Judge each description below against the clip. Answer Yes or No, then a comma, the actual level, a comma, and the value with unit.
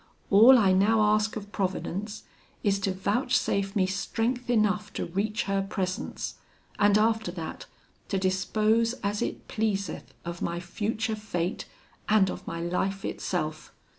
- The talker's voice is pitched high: Yes, high, 200 Hz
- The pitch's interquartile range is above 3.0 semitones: No, narrow, 2.4 semitones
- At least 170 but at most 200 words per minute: No, average, 140 wpm